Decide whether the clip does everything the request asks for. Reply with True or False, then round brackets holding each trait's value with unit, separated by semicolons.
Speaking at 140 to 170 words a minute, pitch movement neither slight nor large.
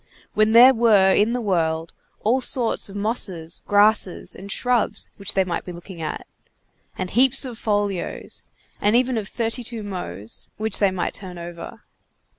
True (155 wpm; 4.1 semitones)